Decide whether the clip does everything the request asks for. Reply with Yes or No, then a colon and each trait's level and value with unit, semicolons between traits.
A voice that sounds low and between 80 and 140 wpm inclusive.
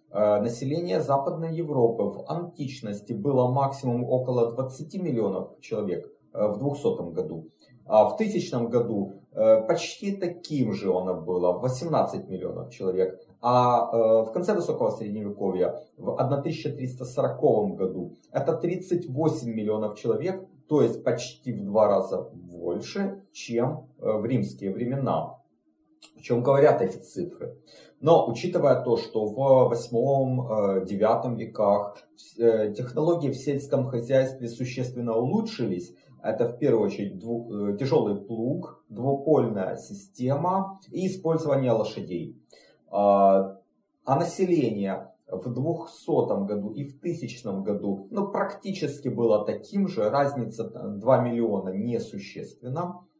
Yes: low, 130 Hz; slow, 110 wpm